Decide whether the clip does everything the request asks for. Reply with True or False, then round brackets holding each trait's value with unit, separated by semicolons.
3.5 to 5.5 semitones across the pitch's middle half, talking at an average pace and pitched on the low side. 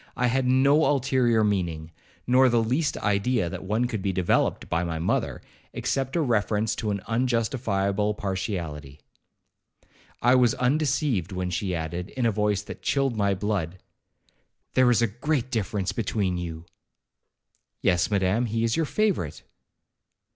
True (5.1 semitones; 145 wpm; 110 Hz)